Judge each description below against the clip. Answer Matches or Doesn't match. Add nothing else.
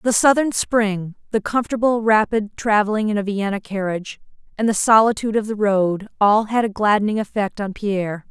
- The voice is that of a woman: Matches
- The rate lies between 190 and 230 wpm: Doesn't match